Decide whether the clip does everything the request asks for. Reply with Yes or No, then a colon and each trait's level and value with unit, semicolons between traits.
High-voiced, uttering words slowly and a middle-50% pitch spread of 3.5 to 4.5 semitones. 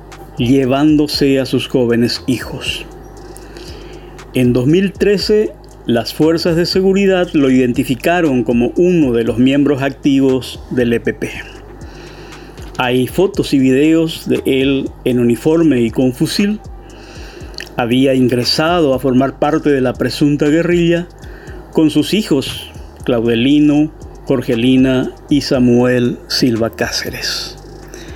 No: low, 135 Hz; slow, 105 wpm; average, 4.2 semitones